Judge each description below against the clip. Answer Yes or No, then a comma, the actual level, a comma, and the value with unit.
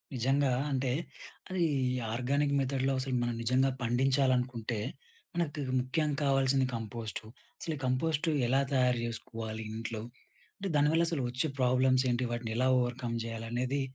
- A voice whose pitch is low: Yes, low, 130 Hz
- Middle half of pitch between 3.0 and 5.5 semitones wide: No, narrow, 2.4 semitones